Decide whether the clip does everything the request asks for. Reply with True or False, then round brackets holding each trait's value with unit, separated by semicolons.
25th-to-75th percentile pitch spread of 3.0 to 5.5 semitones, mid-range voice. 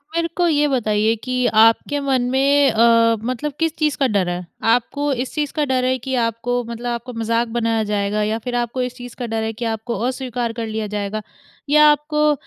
False (3.3 semitones; 240 Hz)